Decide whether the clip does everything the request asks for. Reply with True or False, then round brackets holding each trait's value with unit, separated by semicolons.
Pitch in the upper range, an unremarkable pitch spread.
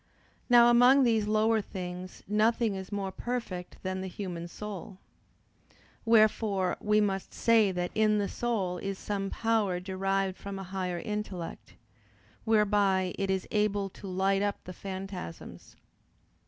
False (195 Hz; 2.3 semitones)